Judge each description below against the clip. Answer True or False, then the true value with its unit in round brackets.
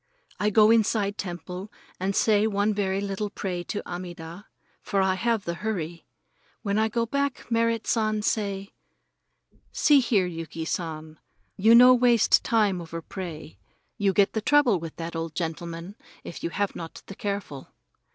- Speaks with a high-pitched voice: True (200 Hz)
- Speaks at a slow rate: False (160 wpm)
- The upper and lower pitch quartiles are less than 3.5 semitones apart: False (4.2 semitones)